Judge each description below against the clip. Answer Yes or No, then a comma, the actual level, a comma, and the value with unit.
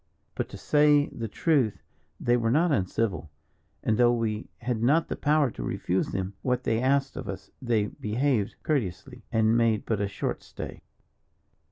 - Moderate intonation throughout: Yes, average, 4.2 semitones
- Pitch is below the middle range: Yes, low, 115 Hz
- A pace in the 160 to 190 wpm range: Yes, average, 170 wpm